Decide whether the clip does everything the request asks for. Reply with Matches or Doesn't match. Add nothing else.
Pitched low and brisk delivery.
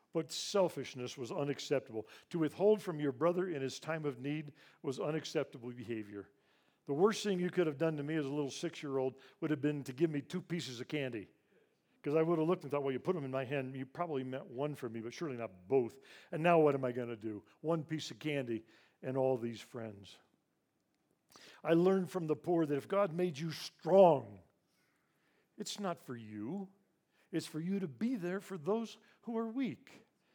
Doesn't match